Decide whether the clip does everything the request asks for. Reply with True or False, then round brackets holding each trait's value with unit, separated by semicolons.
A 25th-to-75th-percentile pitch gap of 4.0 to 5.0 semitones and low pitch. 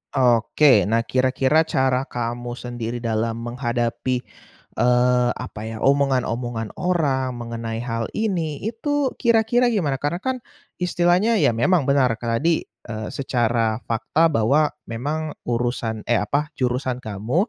True (4.7 semitones; 125 Hz)